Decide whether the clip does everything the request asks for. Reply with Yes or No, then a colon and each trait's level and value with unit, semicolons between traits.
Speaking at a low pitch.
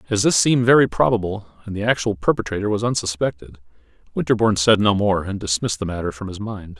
Yes: low, 100 Hz